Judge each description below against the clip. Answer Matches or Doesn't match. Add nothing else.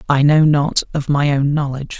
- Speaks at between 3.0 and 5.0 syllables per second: Doesn't match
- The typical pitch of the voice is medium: Matches